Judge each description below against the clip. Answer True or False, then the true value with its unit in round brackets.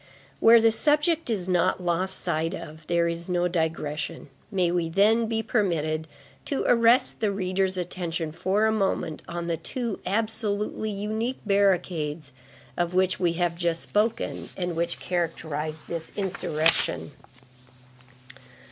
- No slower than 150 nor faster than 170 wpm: False (135 wpm)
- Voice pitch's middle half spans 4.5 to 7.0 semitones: False (4.1 semitones)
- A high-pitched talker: False (180 Hz)